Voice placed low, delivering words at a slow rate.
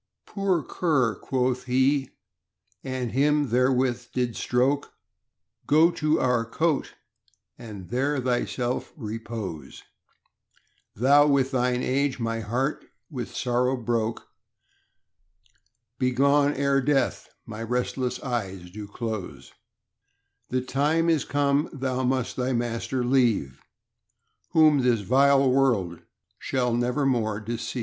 Yes: low, 125 Hz; slow, 110 wpm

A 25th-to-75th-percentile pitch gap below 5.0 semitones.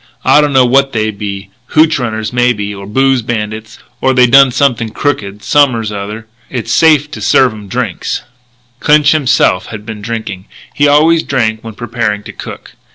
Yes: average, 4.4 semitones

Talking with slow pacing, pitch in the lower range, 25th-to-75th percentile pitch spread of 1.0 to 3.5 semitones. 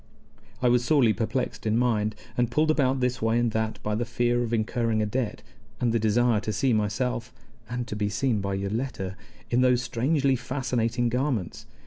No: average, 185 wpm; low, 120 Hz; narrow, 2.5 semitones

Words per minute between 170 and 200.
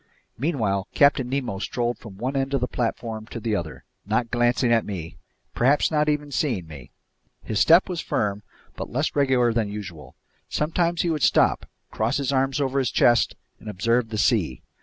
Yes: average, 180 wpm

